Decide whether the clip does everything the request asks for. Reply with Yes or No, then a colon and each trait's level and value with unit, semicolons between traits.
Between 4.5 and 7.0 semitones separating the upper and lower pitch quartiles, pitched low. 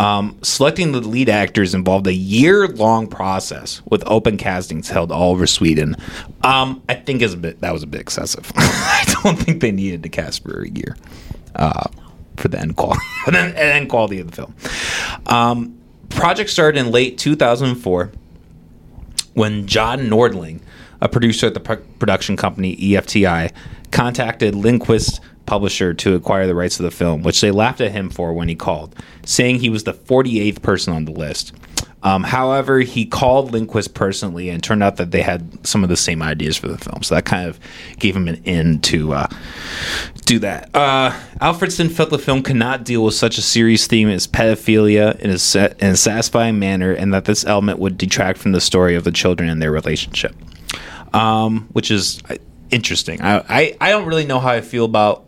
Yes: average, 5.0 semitones; low, 105 Hz